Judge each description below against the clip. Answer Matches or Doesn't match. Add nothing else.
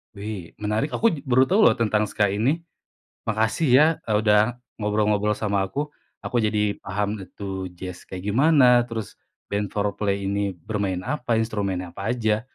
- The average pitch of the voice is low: Matches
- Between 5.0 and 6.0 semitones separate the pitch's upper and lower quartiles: Doesn't match